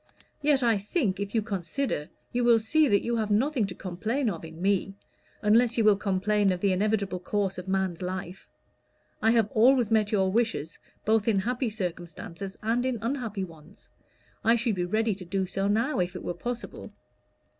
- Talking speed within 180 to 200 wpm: Yes, average, 190 wpm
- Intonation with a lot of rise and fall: No, average, 3.5 semitones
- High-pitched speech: Yes, high, 205 Hz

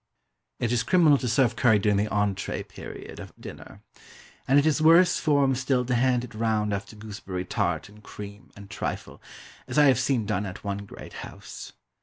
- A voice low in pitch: Yes, low, 115 Hz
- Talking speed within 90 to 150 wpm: No, average, 190 wpm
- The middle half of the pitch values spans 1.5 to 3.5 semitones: No, average, 4.5 semitones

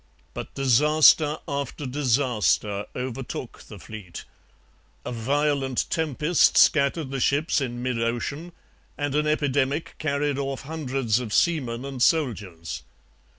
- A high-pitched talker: No, low, 135 Hz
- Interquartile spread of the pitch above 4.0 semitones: No, average, 3.5 semitones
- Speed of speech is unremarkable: No, slow, 115 wpm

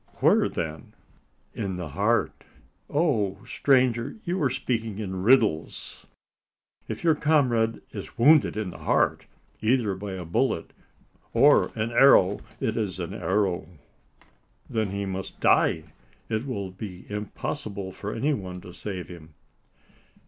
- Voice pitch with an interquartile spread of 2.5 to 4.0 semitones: No, average, 4.5 semitones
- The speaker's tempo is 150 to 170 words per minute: No, slow, 135 wpm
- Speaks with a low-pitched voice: Yes, low, 105 Hz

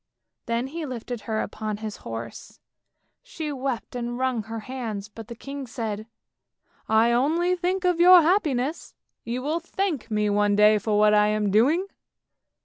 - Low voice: No, high, 240 Hz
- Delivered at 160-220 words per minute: Yes, average, 170 wpm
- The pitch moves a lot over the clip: Yes, wide, 6.0 semitones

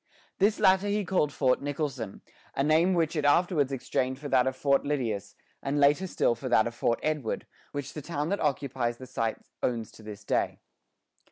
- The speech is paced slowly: No, average, 190 wpm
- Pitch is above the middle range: No, medium, 140 Hz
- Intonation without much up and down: No, average, 3.9 semitones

